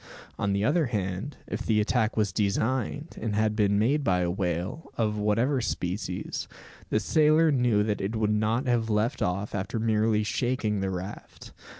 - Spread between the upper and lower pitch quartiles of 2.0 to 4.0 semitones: Yes, average, 2.8 semitones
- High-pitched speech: No, low, 105 Hz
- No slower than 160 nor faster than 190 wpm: Yes, average, 175 wpm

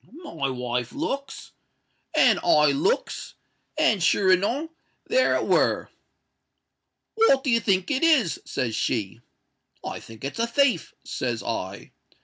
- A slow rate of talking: Yes, slow, 115 wpm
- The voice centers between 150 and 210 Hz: Yes, high, 190 Hz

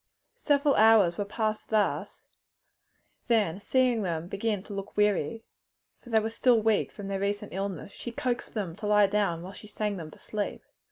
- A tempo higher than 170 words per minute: Yes, average, 180 wpm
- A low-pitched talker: No, high, 210 Hz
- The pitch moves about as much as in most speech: No, narrow, 2.2 semitones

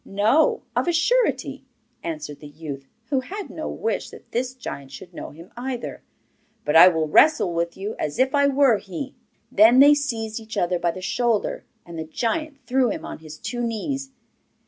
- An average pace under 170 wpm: No, average, 190 wpm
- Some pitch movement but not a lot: No, wide, 8.1 semitones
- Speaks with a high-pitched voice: Yes, high, 225 Hz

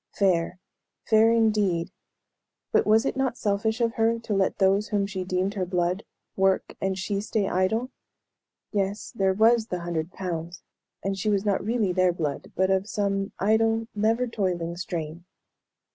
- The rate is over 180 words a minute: No, average, 160 wpm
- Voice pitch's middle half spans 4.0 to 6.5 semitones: No, average, 3.0 semitones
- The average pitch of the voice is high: Yes, high, 195 Hz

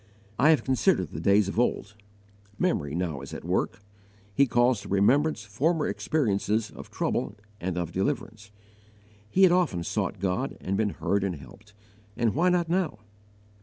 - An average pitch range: No, wide, 6.5 semitones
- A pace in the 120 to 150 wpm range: No, average, 165 wpm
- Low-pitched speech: Yes, low, 105 Hz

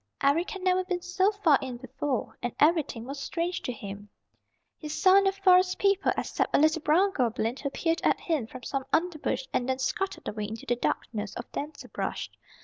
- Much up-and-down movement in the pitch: Yes, wide, 6.5 semitones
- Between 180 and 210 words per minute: Yes, average, 195 wpm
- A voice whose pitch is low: No, very high, 300 Hz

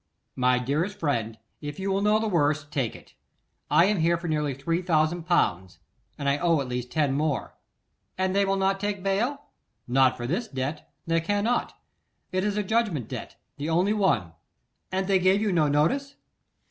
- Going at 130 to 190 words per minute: Yes, average, 185 wpm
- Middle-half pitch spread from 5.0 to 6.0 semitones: Yes, wide, 5.5 semitones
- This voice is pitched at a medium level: Yes, medium, 170 Hz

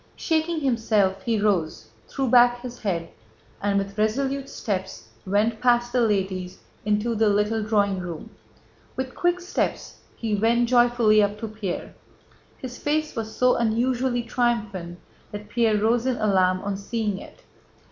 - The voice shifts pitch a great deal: No, average, 3.2 semitones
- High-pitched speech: Yes, high, 220 Hz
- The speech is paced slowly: No, average, 145 wpm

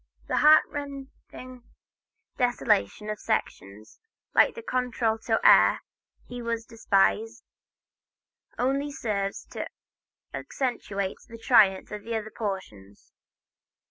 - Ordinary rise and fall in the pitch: Yes, average, 4.0 semitones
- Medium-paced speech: No, slow, 95 wpm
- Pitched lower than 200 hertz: No, high, 225 Hz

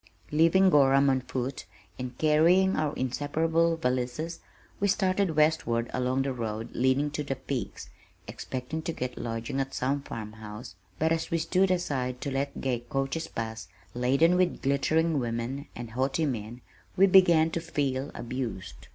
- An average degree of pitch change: Yes, average, 4.5 semitones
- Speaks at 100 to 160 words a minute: Yes, average, 155 wpm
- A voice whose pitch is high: No, low, 135 Hz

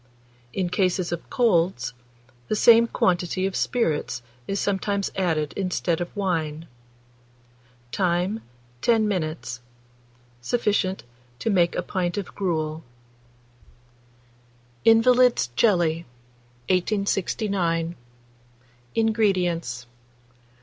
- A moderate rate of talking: No, slow, 85 wpm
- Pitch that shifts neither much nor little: Yes, average, 3.8 semitones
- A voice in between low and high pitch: Yes, medium, 180 Hz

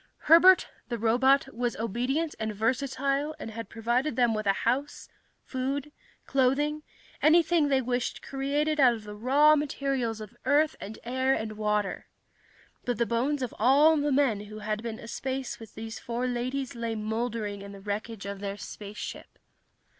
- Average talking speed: Yes, average, 160 wpm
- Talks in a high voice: Yes, high, 245 Hz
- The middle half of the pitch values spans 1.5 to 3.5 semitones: No, average, 4.1 semitones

